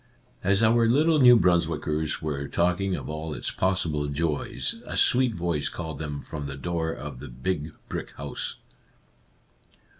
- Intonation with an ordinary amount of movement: Yes, average, 4.2 semitones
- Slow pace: No, average, 155 wpm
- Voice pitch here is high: No, very low, 85 Hz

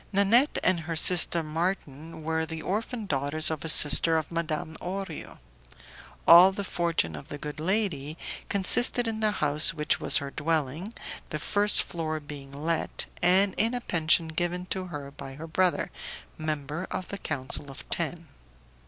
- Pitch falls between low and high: Yes, medium, 165 Hz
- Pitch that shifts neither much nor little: Yes, average, 3.7 semitones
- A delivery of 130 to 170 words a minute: Yes, average, 160 wpm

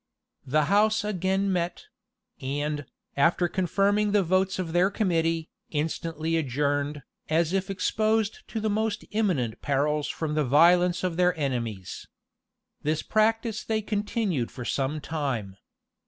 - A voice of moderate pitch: Yes, medium, 170 Hz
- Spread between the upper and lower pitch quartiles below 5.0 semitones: No, wide, 5.4 semitones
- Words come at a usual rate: No, slow, 130 wpm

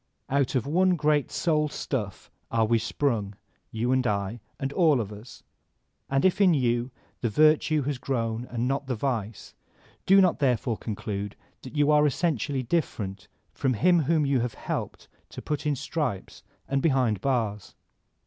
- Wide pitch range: No, average, 4.7 semitones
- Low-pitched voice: Yes, low, 130 Hz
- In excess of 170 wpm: No, average, 165 wpm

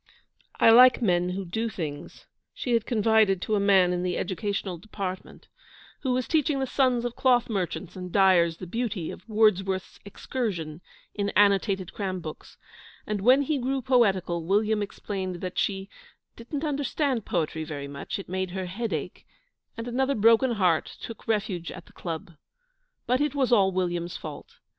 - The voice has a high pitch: Yes, high, 200 Hz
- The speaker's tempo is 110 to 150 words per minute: No, average, 165 wpm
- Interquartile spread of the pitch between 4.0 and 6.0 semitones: Yes, average, 4.7 semitones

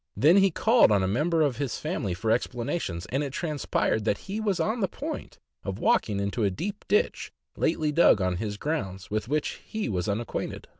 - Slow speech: No, average, 200 wpm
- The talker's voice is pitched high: No, low, 135 Hz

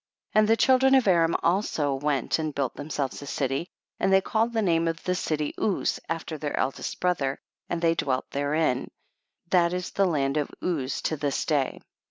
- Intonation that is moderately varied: Yes, average, 4.2 semitones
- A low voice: No, medium, 160 Hz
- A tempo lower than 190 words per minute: No, average, 195 wpm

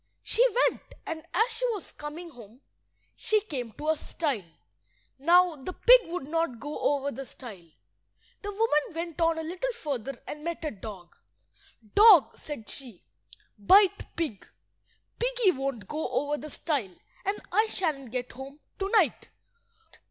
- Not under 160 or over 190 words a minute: No, average, 150 wpm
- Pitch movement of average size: No, wide, 5.9 semitones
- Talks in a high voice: Yes, very high, 310 Hz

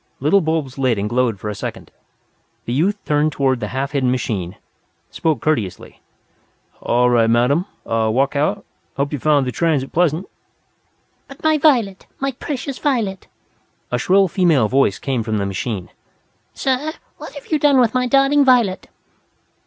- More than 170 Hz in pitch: No, medium, 150 Hz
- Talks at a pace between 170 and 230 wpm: No, average, 160 wpm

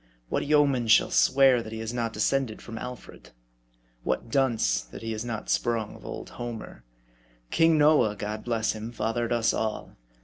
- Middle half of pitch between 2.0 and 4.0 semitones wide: Yes, narrow, 2.4 semitones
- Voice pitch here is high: No, low, 115 Hz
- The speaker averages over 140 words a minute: Yes, average, 170 wpm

